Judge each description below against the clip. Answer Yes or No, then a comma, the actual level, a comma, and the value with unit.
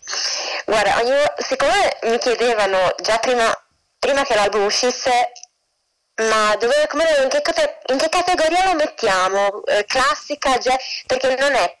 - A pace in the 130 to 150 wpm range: Yes, average, 140 wpm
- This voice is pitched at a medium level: No, very high, 260 Hz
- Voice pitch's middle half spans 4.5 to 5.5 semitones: Yes, average, 5.2 semitones